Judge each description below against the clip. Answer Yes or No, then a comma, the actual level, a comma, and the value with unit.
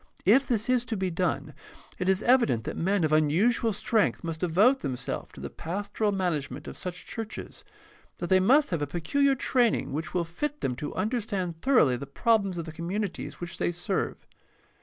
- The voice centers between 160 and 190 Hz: Yes, medium, 185 Hz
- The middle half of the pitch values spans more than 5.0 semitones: Yes, wide, 5.5 semitones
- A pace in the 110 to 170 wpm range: No, average, 200 wpm